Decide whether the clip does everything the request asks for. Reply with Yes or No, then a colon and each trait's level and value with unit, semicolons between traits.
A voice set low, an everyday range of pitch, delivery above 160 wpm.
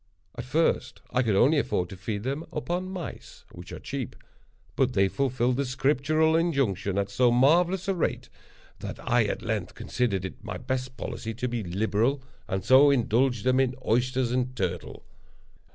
Yes: low, 125 Hz; average, 4.0 semitones; average, 170 wpm